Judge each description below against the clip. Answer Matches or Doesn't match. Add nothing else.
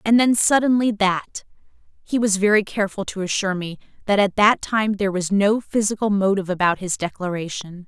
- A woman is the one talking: Matches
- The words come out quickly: Doesn't match